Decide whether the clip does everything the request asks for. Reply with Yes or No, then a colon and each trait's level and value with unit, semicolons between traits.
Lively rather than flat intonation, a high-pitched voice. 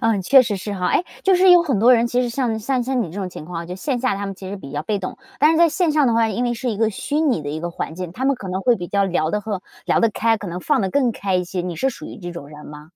Yes: wide, 5.7 semitones; high, 210 Hz